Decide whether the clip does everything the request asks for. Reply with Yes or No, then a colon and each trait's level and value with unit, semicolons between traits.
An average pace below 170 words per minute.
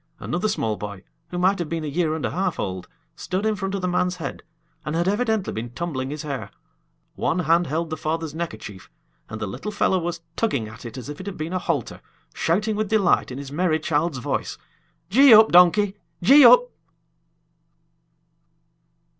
No: average, 190 wpm